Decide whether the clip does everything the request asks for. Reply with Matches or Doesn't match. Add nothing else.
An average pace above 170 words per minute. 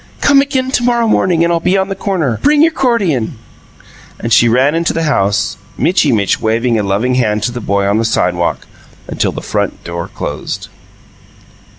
Matches